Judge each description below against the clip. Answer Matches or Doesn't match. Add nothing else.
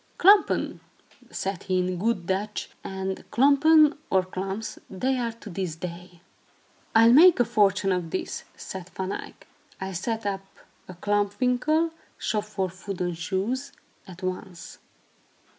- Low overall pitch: Doesn't match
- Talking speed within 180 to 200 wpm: Doesn't match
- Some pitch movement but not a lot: Matches